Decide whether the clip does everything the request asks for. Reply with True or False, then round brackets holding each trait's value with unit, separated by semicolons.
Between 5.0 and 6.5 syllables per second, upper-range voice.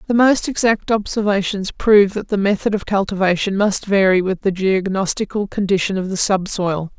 True (5.2 syllables/s; 195 Hz)